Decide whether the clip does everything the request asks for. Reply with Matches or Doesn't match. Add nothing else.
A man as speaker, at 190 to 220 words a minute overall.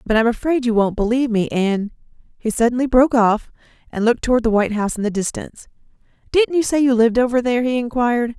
Doesn't match